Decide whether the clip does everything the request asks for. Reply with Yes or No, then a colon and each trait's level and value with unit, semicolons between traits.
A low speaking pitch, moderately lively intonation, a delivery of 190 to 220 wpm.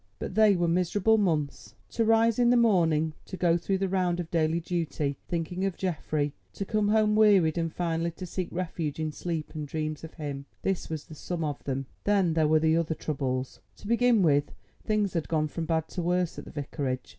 No: medium, 170 Hz; average, 3.8 semitones; average, 200 wpm